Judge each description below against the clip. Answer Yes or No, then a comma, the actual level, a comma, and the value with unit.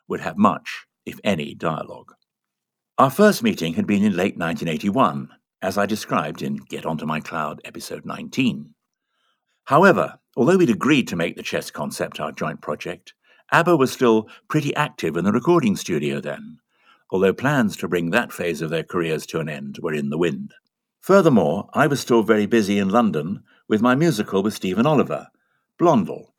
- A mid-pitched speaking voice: No, low, 130 Hz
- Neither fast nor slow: Yes, average, 175 wpm